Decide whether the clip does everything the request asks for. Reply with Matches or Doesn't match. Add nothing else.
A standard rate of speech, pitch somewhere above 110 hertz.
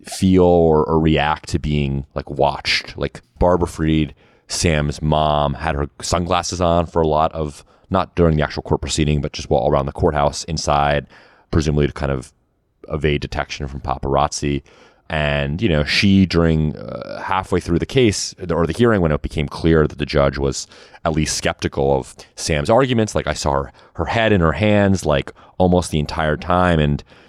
Doesn't match